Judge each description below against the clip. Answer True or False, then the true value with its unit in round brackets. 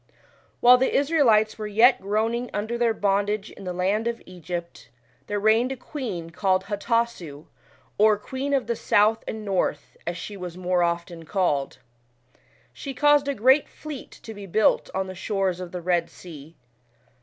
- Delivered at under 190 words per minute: True (170 wpm)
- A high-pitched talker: True (205 Hz)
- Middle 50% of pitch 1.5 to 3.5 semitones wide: False (4.4 semitones)